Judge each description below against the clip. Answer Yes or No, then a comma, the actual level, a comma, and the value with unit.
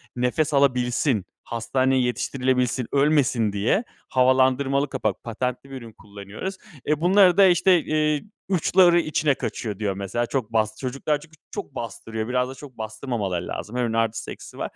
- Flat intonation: No, average, 4.5 semitones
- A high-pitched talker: No, low, 130 Hz